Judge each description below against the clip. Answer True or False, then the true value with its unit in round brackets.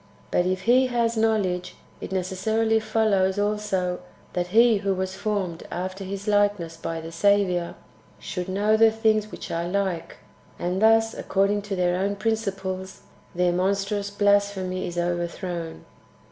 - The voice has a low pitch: False (195 Hz)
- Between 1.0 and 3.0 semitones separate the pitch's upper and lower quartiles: True (2.7 semitones)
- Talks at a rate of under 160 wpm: True (145 wpm)